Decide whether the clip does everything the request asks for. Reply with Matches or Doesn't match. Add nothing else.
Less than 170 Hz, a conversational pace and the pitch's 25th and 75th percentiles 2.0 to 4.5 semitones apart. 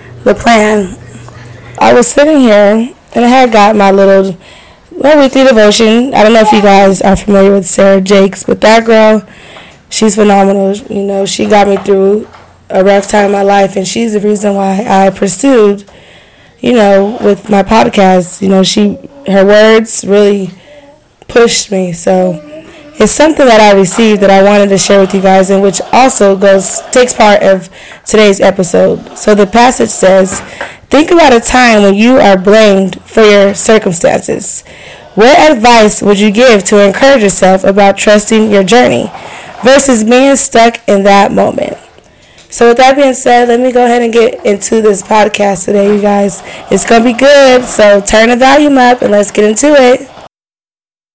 Doesn't match